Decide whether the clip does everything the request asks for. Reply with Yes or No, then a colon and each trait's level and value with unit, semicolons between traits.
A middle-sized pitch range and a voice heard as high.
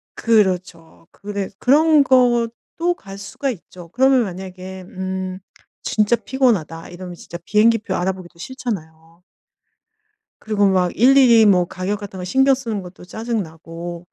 Yes: average, 4.8 semitones; high, 195 Hz